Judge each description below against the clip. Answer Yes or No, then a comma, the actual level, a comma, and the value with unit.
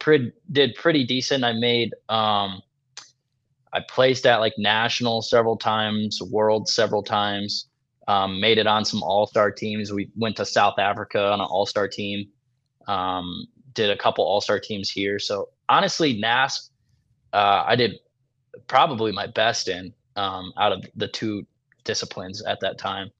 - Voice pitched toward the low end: Yes, low, 110 Hz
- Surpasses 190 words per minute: No, average, 160 wpm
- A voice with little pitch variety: No, average, 3.9 semitones